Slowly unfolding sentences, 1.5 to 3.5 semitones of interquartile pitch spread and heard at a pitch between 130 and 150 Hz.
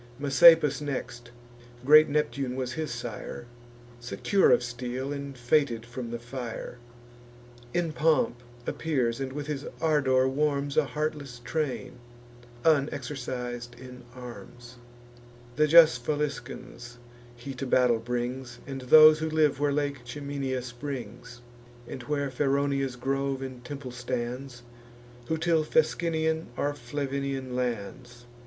Yes: slow, 120 wpm; average, 3.1 semitones; low, 135 Hz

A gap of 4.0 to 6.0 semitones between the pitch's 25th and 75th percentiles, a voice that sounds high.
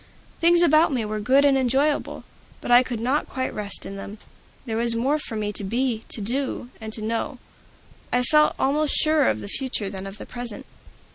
Yes: average, 4.4 semitones; high, 245 Hz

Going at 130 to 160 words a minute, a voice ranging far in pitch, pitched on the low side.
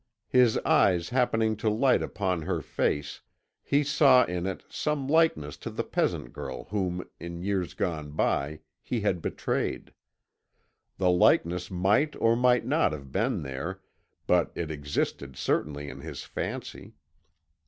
Yes: average, 145 wpm; wide, 7.8 semitones; very low, 90 Hz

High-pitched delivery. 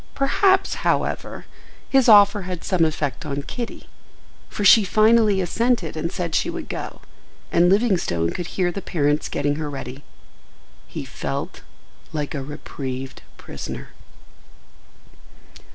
No: medium, 175 Hz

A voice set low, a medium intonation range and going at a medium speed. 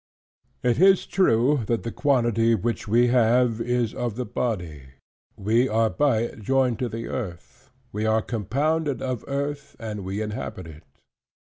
Yes: low, 115 Hz; average, 3.0 semitones; average, 155 wpm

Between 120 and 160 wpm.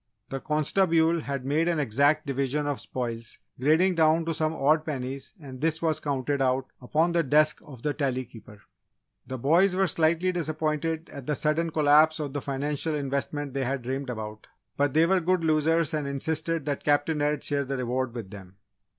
No: average, 185 wpm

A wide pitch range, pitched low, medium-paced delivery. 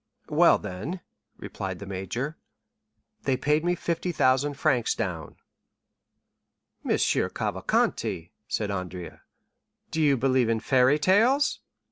No: wide, 7.7 semitones; low, 130 Hz; slow, 105 wpm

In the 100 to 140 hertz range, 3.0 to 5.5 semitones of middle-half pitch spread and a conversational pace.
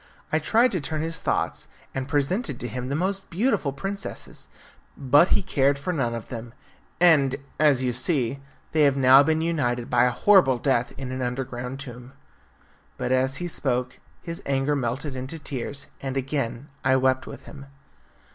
Yes: low, 135 Hz; average, 3.6 semitones; average, 175 wpm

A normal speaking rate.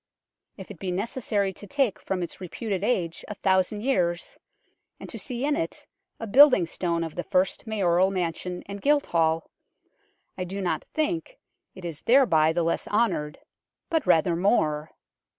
Yes: average, 160 wpm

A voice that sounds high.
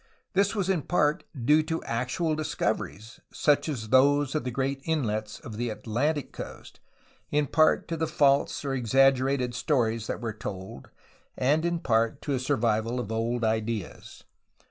No: low, 130 Hz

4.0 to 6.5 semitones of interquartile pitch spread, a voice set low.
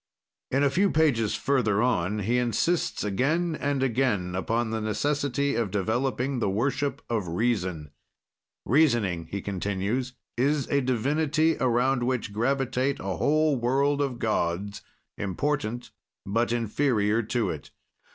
Yes: average, 5.1 semitones; low, 120 Hz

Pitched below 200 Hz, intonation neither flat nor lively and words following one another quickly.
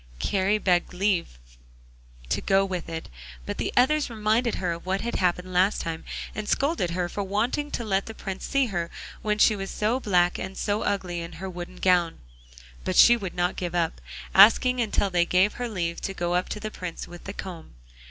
Yes: high, 190 Hz; average, 3.3 semitones; fast, 210 wpm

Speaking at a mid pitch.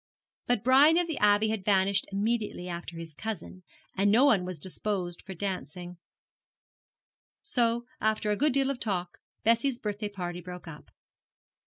No: high, 205 Hz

